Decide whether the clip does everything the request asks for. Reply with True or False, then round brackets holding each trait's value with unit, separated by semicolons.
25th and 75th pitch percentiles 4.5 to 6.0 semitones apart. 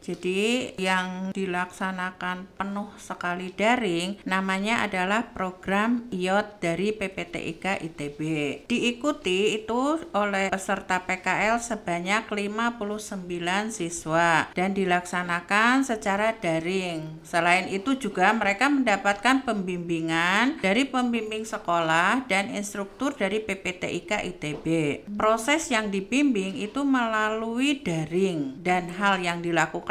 False (3.3 semitones)